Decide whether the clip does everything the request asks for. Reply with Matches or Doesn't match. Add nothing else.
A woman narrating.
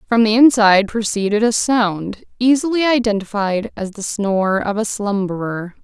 Matches